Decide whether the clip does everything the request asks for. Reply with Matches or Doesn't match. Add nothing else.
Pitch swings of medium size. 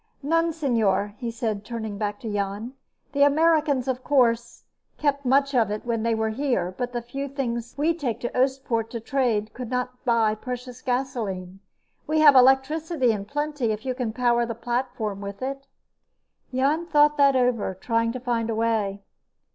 Matches